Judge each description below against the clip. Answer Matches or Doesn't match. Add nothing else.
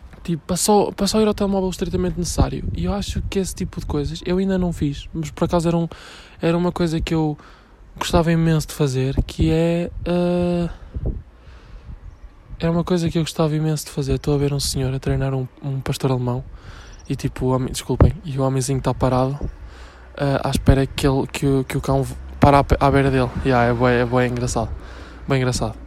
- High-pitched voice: Doesn't match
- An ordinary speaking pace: Doesn't match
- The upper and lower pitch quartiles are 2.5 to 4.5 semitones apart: Doesn't match